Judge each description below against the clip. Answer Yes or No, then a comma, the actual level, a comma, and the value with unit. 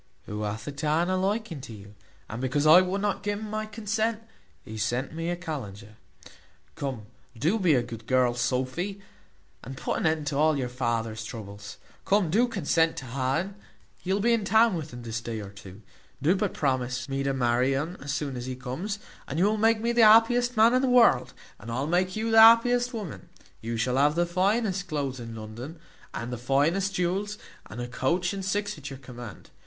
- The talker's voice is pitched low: No, medium, 150 Hz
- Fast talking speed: Yes, fast, 210 wpm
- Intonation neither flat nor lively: No, wide, 8.3 semitones